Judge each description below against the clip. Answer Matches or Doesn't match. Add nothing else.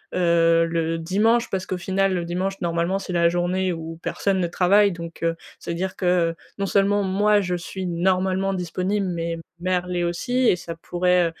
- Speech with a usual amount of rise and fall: Doesn't match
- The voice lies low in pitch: Doesn't match